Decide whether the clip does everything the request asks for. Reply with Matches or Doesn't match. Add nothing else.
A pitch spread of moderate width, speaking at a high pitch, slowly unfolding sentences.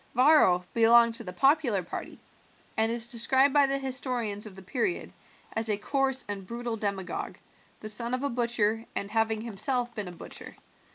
Doesn't match